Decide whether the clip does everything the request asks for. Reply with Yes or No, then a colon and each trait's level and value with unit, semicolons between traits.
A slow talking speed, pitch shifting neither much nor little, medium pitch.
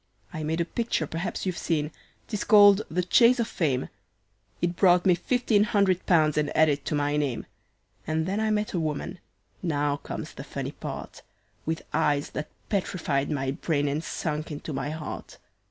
No: average, 175 wpm; average, 4.3 semitones; medium, 160 Hz